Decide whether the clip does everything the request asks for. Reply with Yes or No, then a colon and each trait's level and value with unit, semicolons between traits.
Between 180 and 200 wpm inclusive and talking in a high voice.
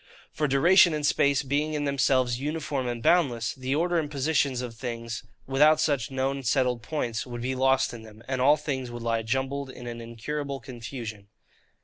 No: average, 185 wpm; low, 130 Hz